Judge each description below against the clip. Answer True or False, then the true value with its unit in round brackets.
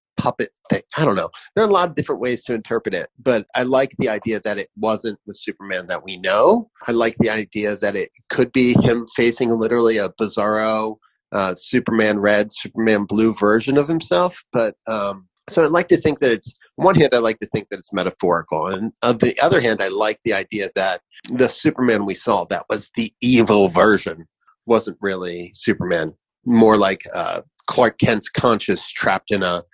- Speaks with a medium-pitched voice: False (110 Hz)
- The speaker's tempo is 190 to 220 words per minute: True (200 wpm)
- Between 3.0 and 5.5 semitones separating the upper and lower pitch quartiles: False (2.5 semitones)